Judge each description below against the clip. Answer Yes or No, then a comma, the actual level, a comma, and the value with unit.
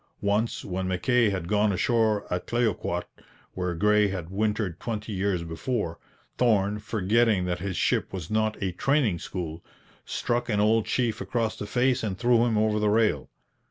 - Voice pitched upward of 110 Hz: No, low, 105 Hz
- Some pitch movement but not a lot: Yes, average, 3.4 semitones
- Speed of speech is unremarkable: Yes, average, 165 wpm